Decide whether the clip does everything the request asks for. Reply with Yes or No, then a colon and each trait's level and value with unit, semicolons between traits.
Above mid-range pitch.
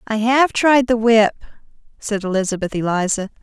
Yes: high, 220 Hz